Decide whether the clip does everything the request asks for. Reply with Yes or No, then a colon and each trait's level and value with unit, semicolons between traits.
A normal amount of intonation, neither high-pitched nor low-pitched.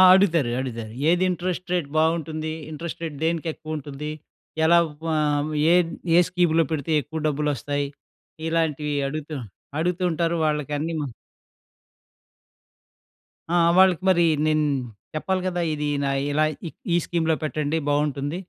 No: narrow, 2.3 semitones; medium, 155 Hz